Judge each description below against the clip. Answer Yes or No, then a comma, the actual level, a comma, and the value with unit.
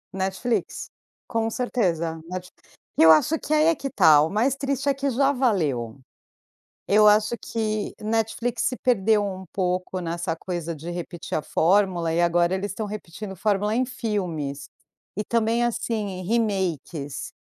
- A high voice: Yes, high, 200 Hz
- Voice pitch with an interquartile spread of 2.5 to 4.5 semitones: No, average, 4.9 semitones